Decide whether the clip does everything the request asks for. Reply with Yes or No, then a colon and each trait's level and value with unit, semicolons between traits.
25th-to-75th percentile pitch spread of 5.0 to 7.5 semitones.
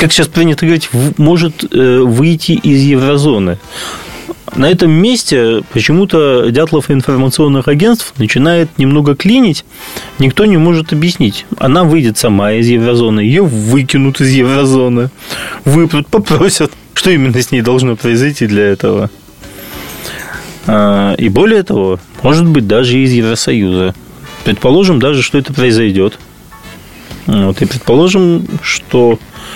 Yes: wide, 5.5 semitones